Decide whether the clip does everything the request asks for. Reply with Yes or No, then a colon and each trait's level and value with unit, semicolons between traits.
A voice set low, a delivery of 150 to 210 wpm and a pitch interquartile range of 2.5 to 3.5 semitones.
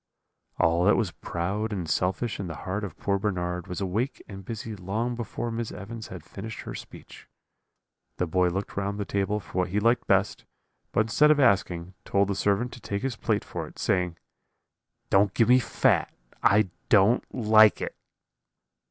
Yes: low, 100 Hz; average, 180 wpm; average, 3.2 semitones